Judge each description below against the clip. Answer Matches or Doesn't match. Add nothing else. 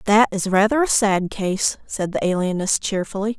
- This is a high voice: Matches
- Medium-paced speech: Matches